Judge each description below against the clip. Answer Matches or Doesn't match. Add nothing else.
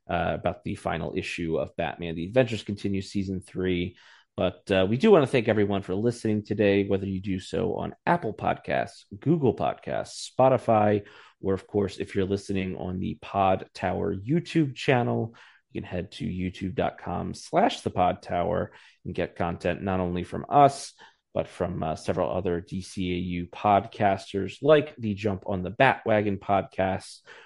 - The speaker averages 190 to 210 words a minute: Doesn't match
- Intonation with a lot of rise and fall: Doesn't match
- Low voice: Matches